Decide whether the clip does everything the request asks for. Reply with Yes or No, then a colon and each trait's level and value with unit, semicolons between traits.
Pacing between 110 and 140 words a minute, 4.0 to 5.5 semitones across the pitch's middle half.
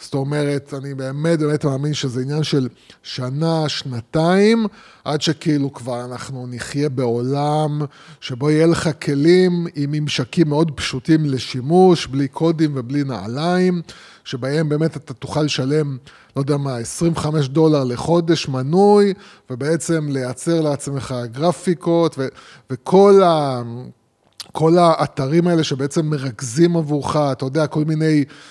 No: average, 125 wpm; average, 3.5 semitones